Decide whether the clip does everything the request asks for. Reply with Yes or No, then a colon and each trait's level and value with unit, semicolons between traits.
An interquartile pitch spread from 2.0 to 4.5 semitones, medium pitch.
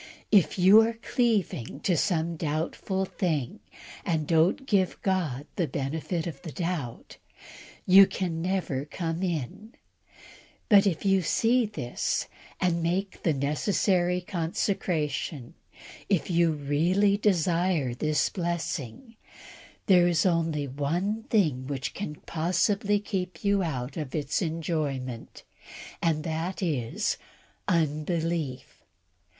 Yes: average, 4.1 semitones; medium, 170 Hz